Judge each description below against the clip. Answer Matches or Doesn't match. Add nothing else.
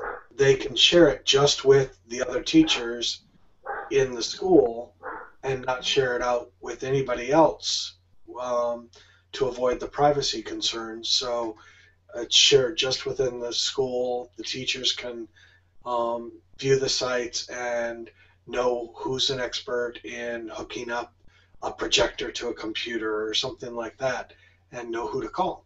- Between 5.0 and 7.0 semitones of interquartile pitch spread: Doesn't match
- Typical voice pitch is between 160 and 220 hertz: Doesn't match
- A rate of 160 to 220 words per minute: Doesn't match